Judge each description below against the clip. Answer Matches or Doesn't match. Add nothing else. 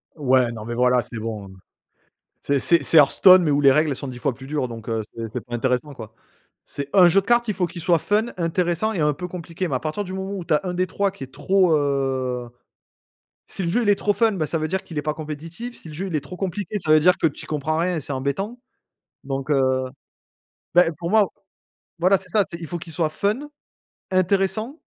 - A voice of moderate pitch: Matches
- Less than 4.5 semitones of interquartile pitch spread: Doesn't match